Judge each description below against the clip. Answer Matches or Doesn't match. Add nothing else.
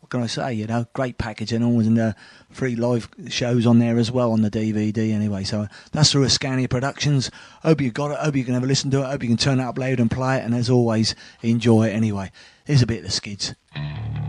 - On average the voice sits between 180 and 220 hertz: Doesn't match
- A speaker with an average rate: Doesn't match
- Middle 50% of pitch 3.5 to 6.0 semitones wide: Doesn't match